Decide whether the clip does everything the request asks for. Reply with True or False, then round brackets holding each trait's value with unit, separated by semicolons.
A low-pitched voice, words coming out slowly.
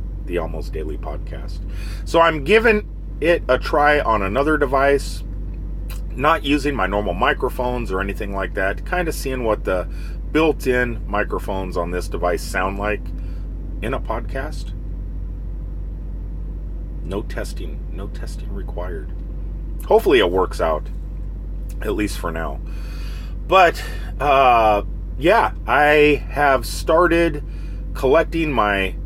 True (95 Hz; 120 wpm)